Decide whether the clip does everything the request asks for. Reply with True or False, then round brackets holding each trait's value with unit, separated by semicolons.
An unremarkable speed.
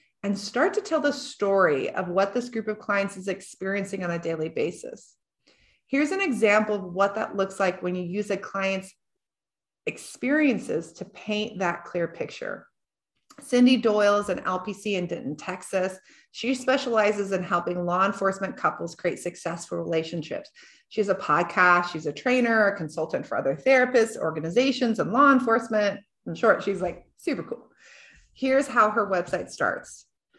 True (160 wpm)